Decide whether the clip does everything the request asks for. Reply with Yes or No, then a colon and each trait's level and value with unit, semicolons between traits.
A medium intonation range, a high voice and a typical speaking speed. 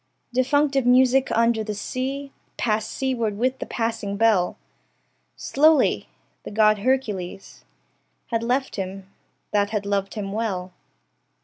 No: average, 4.3 semitones; high, 225 Hz; slow, 115 wpm